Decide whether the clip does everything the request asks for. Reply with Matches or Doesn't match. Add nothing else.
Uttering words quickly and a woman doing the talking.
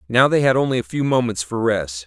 Doesn't match